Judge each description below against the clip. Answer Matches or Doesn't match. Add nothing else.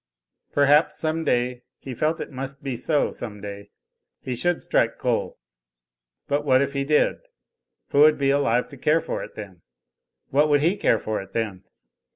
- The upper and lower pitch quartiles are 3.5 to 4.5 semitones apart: Matches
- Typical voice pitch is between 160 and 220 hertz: Doesn't match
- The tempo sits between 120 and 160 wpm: Doesn't match